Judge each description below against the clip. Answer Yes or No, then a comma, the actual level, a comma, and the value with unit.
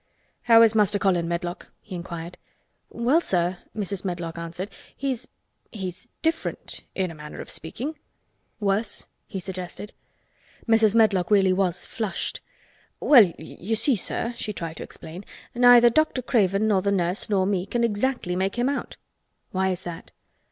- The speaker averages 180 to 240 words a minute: No, average, 150 wpm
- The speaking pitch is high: Yes, high, 195 Hz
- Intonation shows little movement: No, average, 4.3 semitones